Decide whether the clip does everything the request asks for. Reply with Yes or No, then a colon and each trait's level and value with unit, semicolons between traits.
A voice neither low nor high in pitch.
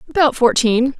No: very high, 260 Hz